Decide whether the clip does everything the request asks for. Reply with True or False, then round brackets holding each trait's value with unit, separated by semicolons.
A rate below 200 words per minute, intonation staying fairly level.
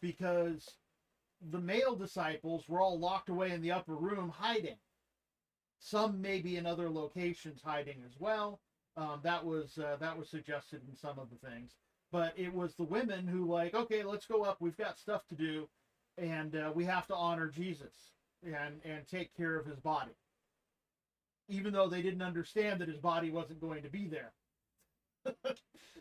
False (175 wpm; 3.2 semitones)